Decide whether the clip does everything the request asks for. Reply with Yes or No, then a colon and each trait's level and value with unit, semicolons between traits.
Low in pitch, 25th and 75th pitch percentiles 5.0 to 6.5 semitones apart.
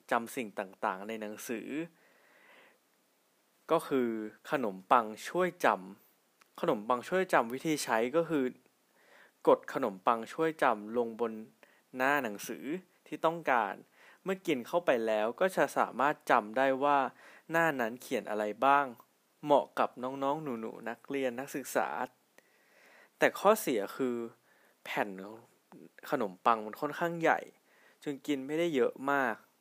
Yes: low, 130 Hz; wide, 5.6 semitones